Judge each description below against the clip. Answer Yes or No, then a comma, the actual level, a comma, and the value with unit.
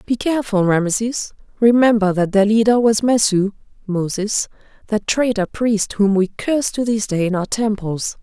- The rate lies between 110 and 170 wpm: Yes, average, 160 wpm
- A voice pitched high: Yes, high, 210 Hz